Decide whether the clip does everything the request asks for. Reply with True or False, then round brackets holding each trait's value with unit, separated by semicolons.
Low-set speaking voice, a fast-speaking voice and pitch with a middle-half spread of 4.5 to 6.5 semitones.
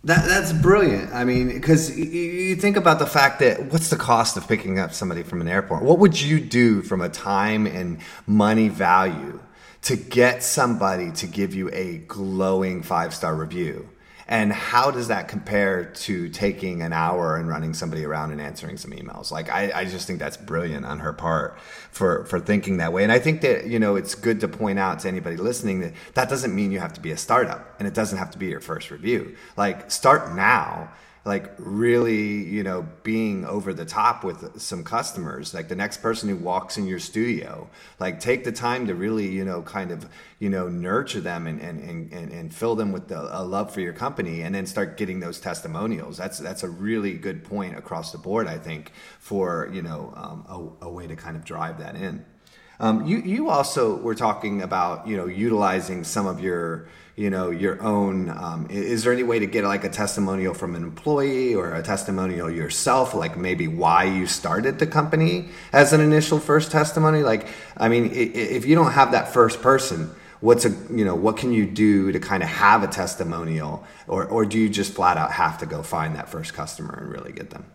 True (105 Hz; 215 wpm; 5.6 semitones)